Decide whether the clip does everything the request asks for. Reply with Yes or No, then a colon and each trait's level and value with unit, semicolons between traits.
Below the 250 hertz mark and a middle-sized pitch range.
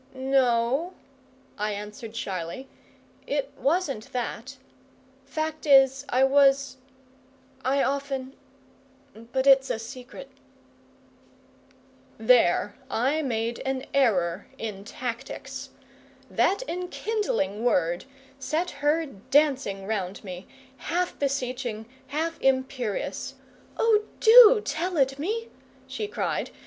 No: very high, 265 Hz; average, 4.6 semitones